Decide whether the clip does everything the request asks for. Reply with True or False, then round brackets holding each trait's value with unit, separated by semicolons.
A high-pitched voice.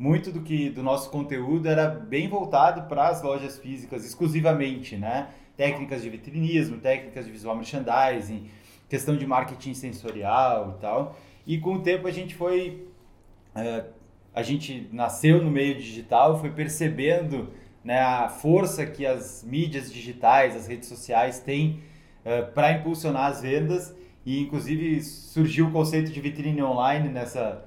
False (140 Hz)